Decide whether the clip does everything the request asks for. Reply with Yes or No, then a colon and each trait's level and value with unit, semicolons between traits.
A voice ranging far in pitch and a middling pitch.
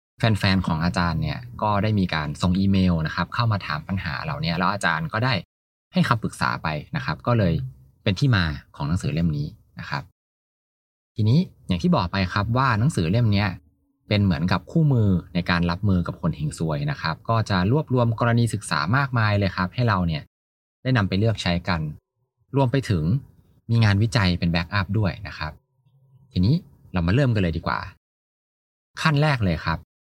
No: wide, 6.6 semitones; low, 100 Hz